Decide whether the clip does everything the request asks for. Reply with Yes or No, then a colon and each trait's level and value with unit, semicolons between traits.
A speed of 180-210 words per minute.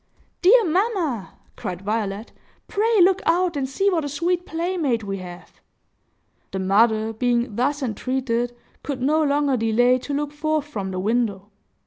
No: average, 150 wpm